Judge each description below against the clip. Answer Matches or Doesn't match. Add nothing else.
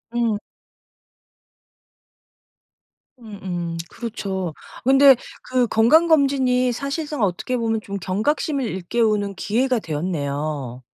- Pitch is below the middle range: Doesn't match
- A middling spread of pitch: Doesn't match